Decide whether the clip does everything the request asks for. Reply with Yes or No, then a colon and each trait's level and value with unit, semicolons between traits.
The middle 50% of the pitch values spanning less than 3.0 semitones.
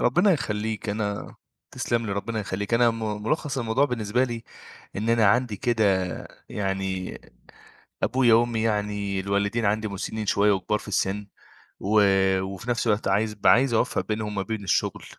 Yes: narrow, 2.4 semitones